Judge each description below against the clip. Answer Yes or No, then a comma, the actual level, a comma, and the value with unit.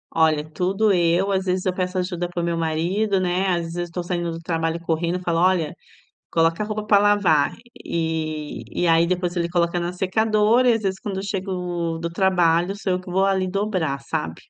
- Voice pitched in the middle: Yes, medium, 180 Hz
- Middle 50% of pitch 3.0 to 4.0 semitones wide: No, narrow, 2.4 semitones